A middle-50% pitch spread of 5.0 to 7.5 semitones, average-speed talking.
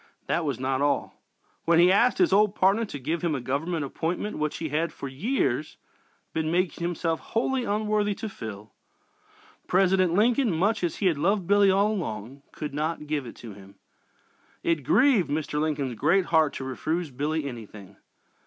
Yes: wide, 5.6 semitones; average, 175 wpm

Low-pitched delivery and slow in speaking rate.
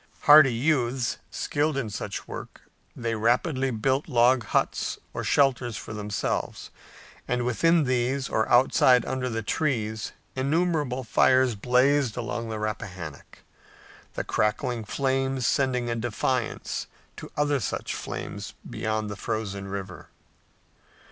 Yes: low, 125 Hz; slow, 120 wpm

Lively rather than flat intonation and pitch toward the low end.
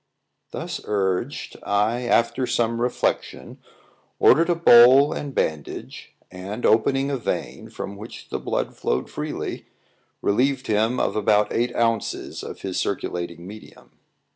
No: average, 3.8 semitones; low, 115 Hz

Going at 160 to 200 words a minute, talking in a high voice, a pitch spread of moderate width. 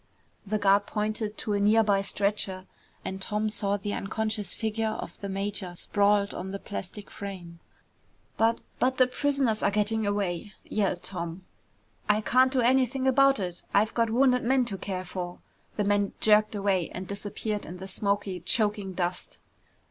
No: average, 165 wpm; high, 205 Hz; narrow, 2.2 semitones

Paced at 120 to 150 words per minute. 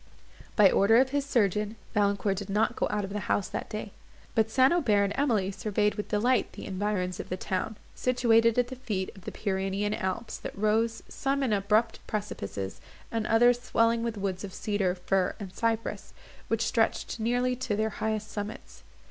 No: average, 185 wpm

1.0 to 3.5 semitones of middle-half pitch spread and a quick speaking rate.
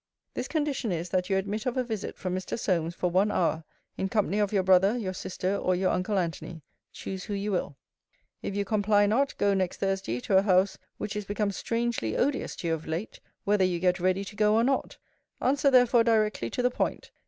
Yes: average, 3.0 semitones; fast, 220 wpm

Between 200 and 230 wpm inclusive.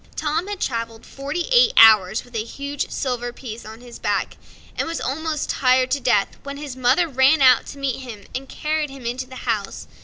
Yes: fast, 205 wpm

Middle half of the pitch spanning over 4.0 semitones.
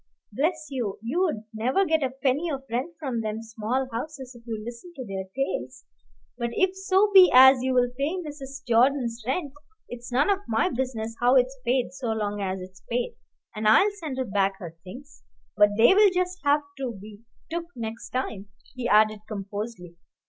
Yes: average, 4.6 semitones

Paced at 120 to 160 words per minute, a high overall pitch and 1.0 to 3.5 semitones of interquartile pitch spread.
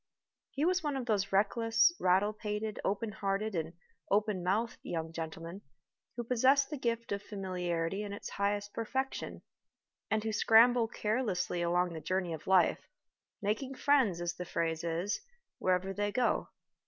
No: average, 155 wpm; high, 205 Hz; average, 4.1 semitones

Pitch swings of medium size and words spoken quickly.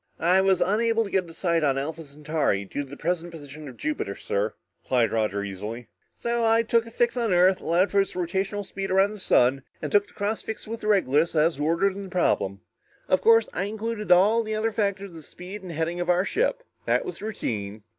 No: wide, 5.7 semitones; fast, 225 wpm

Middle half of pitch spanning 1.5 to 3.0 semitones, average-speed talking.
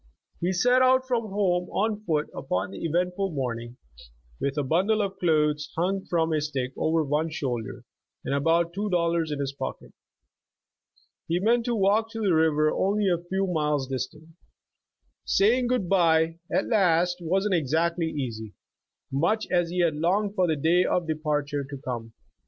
No: average, 4.5 semitones; average, 170 wpm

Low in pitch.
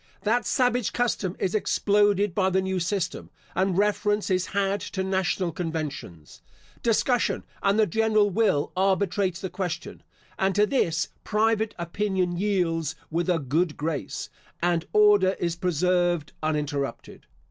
No: high, 190 Hz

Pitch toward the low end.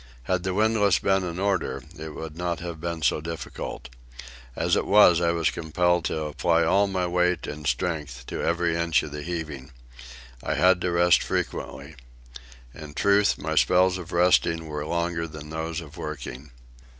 Yes: very low, 85 Hz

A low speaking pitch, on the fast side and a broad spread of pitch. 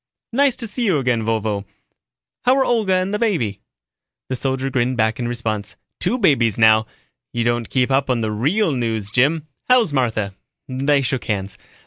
No: low, 125 Hz; average, 170 wpm; wide, 6.8 semitones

